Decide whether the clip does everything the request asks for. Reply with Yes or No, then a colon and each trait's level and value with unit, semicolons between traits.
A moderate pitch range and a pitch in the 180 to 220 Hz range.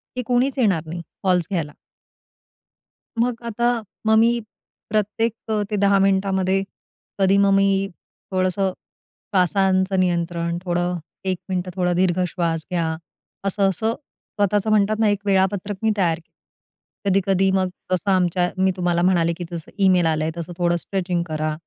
No: narrow, 2.3 semitones; high, 190 Hz